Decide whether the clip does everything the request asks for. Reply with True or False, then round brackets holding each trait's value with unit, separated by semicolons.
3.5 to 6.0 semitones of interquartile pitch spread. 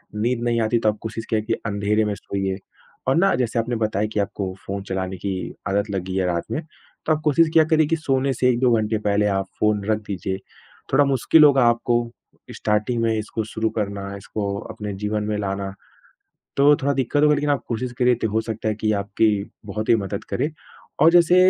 True (4.0 semitones)